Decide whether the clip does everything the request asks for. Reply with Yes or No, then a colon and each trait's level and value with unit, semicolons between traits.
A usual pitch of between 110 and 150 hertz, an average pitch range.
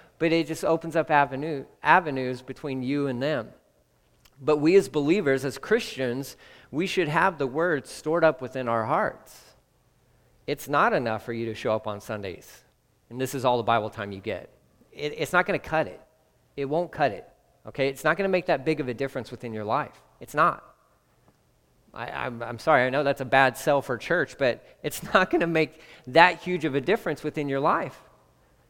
Yes: medium, 140 Hz; average, 4.3 semitones